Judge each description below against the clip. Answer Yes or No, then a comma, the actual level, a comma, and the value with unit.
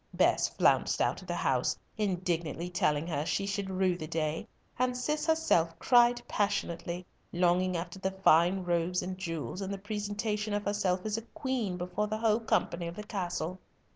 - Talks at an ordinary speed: Yes, average, 175 wpm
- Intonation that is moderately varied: Yes, average, 3.4 semitones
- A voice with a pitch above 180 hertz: Yes, high, 190 Hz